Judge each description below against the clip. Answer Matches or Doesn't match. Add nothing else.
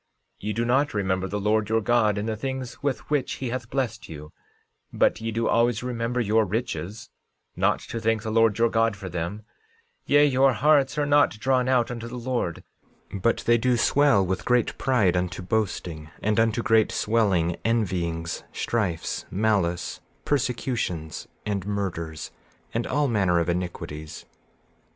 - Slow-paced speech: Doesn't match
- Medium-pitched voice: Doesn't match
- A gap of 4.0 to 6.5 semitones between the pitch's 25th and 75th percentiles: Matches